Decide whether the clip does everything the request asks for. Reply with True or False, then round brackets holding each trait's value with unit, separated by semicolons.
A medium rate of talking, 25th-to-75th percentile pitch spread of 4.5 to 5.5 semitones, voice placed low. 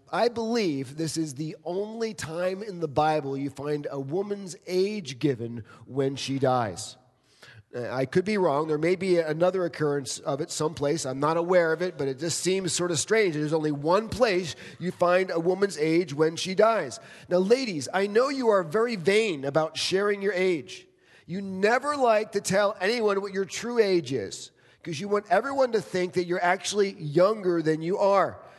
False (190 wpm; 4.9 semitones; 180 Hz)